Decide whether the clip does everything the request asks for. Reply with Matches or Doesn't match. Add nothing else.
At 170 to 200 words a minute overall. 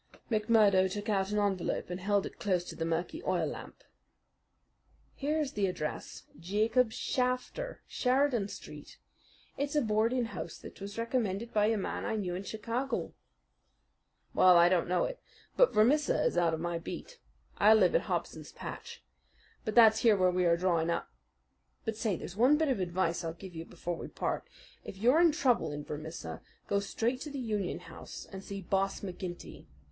Matches